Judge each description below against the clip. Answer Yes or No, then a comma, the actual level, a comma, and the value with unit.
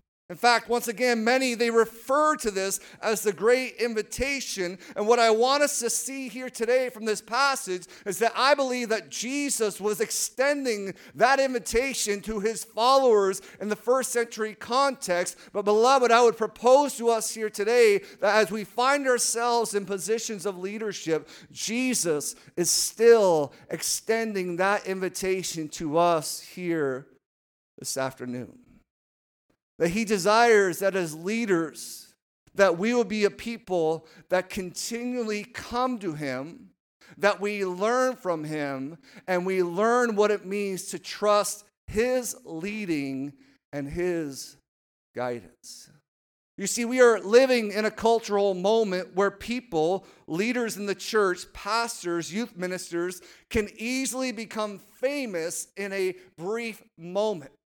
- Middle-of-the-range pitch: No, high, 210 Hz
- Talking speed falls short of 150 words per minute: Yes, average, 140 wpm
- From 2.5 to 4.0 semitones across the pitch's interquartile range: No, average, 4.7 semitones